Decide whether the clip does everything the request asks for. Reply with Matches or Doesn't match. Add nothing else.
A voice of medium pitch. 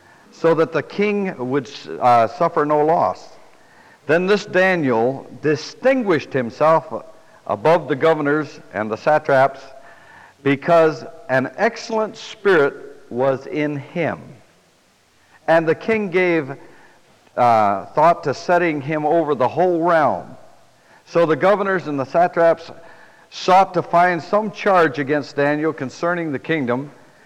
Matches